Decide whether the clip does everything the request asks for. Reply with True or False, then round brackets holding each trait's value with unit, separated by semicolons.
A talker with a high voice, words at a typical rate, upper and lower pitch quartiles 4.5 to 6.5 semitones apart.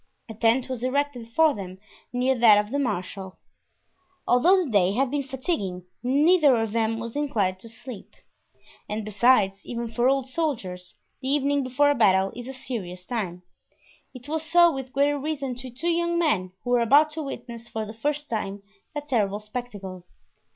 True (245 Hz; 180 wpm; 5.2 semitones)